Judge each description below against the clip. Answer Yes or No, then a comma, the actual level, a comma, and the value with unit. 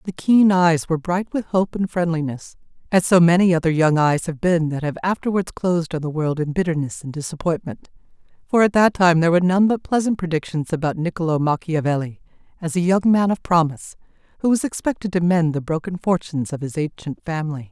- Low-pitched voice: No, medium, 170 Hz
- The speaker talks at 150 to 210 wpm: Yes, average, 200 wpm